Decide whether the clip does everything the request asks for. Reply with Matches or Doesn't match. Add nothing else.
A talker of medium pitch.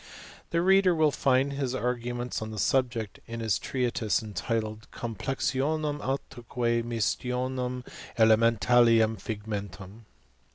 Doesn't match